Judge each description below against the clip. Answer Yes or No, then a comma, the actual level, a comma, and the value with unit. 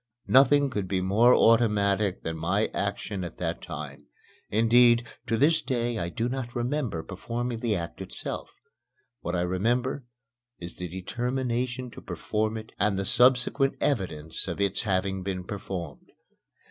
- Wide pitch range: No, average, 4.7 semitones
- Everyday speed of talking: Yes, average, 145 wpm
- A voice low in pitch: Yes, low, 110 Hz